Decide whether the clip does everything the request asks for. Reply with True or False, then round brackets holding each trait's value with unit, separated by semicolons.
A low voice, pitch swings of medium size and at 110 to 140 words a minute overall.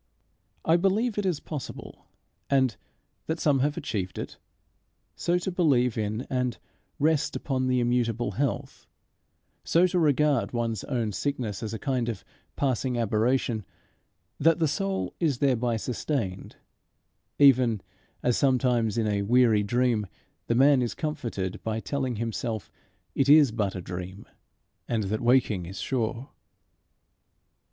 True (125 Hz; 4.3 semitones; 135 wpm)